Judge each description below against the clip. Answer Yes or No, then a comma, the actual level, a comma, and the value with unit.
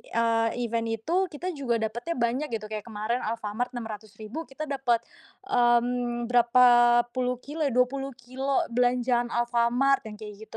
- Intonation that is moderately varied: No, narrow, 2.2 semitones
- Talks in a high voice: Yes, high, 240 Hz